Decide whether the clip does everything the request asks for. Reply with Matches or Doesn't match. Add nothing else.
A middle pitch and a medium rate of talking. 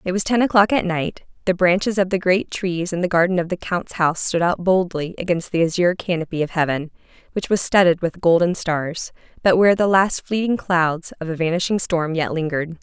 Doesn't match